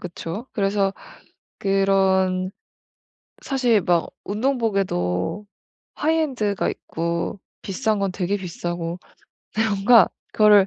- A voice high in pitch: Yes, high, 195 Hz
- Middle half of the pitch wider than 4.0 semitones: No, average, 2.9 semitones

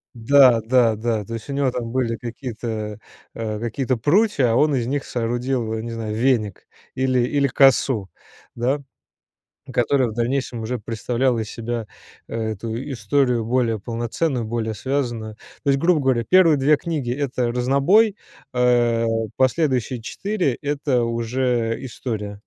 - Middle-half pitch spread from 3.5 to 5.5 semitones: No, average, 3.0 semitones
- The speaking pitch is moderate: No, low, 120 Hz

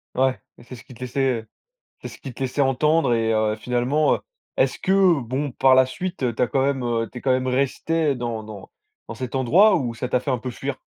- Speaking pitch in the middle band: No, low, 130 Hz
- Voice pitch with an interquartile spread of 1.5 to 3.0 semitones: Yes, narrow, 2.5 semitones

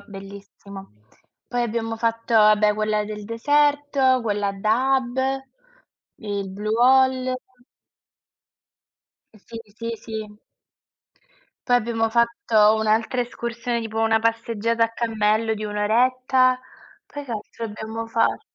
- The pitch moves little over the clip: Yes, narrow, 2.3 semitones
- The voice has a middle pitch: No, high, 225 Hz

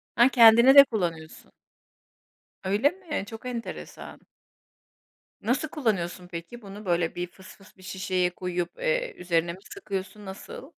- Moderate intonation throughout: No, wide, 5.7 semitones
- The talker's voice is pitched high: Yes, high, 195 Hz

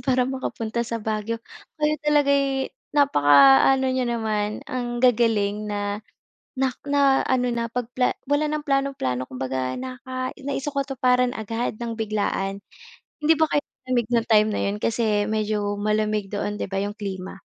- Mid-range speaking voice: No, high, 230 Hz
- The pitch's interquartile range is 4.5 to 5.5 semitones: No, average, 4.1 semitones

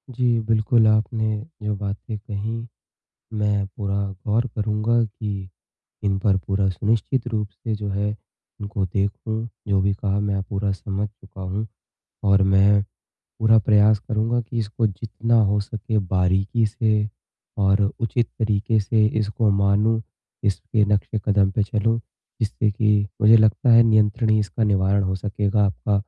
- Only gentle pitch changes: Yes, narrow, 1.9 semitones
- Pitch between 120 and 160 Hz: No, low, 105 Hz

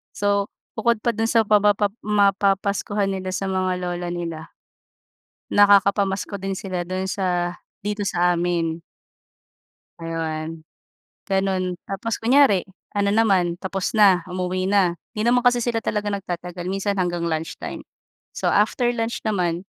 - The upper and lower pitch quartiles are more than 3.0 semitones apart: No, average, 2.7 semitones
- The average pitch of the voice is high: Yes, high, 195 Hz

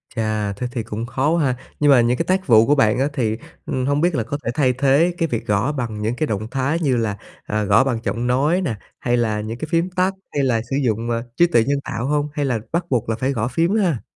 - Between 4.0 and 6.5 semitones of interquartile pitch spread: Yes, average, 4.6 semitones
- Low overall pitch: Yes, low, 125 Hz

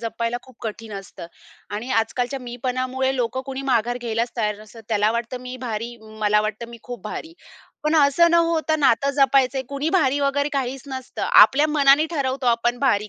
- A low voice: No, very high, 255 Hz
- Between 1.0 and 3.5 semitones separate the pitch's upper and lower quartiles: Yes, average, 3.2 semitones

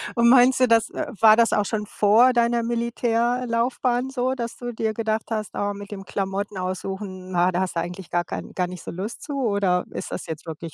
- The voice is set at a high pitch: Yes, high, 215 Hz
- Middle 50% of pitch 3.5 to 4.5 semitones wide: Yes, average, 4.1 semitones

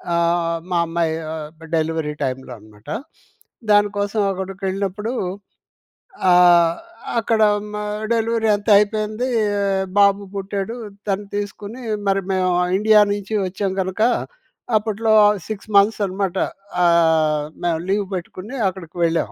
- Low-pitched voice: No, high, 195 Hz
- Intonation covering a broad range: No, average, 3.7 semitones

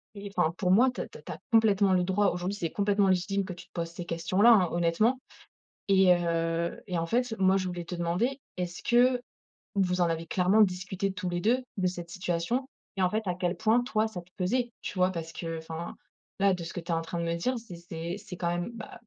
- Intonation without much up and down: No, average, 3.1 semitones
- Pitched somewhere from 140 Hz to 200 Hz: Yes, medium, 185 Hz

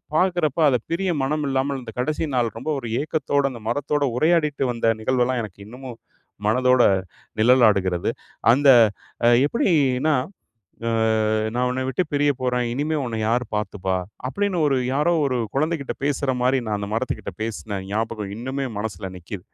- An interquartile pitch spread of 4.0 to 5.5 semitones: Yes, average, 4.4 semitones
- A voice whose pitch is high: No, low, 125 Hz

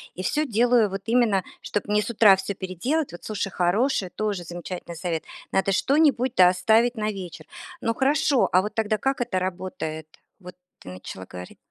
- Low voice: No, high, 200 Hz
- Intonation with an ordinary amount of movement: Yes, average, 4.6 semitones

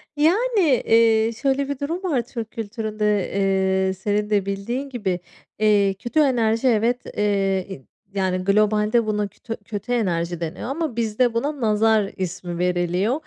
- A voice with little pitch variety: No, average, 3.8 semitones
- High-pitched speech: Yes, high, 215 Hz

